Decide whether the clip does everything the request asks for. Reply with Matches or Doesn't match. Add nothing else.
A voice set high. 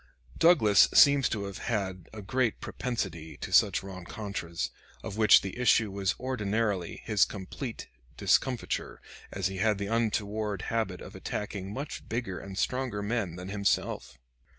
Doesn't match